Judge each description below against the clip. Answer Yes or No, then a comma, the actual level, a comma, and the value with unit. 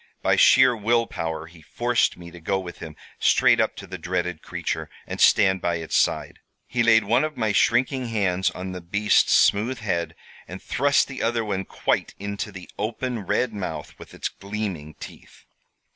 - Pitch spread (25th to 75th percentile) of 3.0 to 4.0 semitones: No, average, 4.7 semitones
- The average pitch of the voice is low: Yes, low, 100 Hz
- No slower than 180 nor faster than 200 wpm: Yes, average, 185 wpm